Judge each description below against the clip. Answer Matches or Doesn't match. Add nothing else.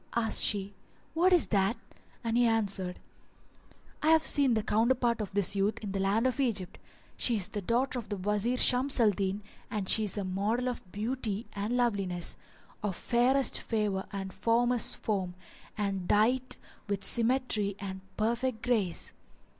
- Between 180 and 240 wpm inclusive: Doesn't match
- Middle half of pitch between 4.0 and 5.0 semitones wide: Doesn't match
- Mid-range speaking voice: Doesn't match